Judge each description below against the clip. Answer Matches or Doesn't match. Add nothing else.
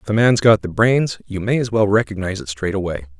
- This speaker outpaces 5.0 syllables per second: Matches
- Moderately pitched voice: Doesn't match